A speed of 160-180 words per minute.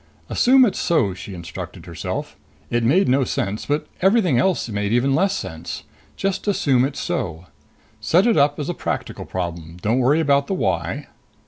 Yes: average, 175 wpm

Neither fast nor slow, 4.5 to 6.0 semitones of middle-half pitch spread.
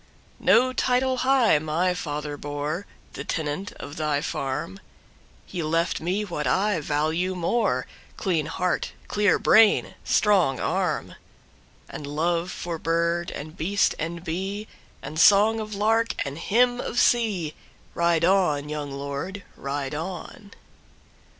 No: slow, 110 wpm; average, 5.2 semitones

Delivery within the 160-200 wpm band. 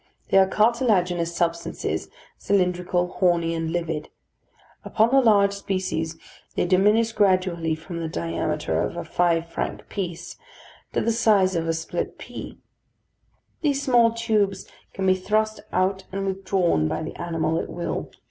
No: average, 145 wpm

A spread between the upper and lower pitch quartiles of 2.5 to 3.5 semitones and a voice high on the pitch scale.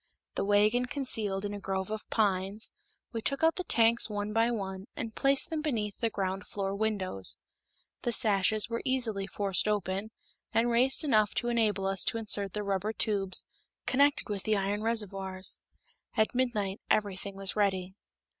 Yes: average, 2.9 semitones; high, 210 Hz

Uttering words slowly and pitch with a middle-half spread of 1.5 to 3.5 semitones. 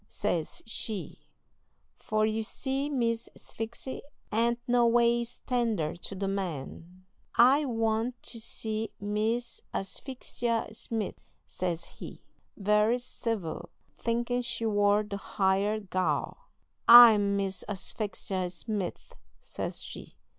Yes: slow, 110 wpm; average, 3.1 semitones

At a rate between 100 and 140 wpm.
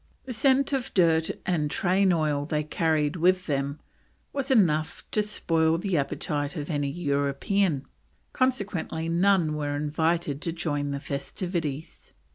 Yes: slow, 135 wpm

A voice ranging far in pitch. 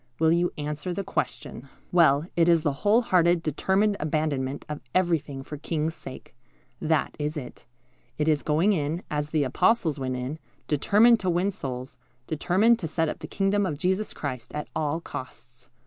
No: average, 3.8 semitones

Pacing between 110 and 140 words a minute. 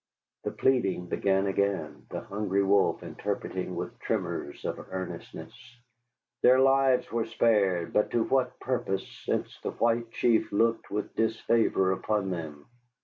Yes: slow, 135 wpm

